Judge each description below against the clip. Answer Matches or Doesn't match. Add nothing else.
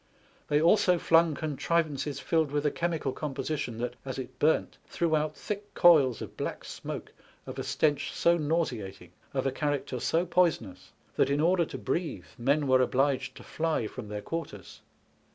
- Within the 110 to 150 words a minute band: Doesn't match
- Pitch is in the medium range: Matches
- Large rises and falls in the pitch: Doesn't match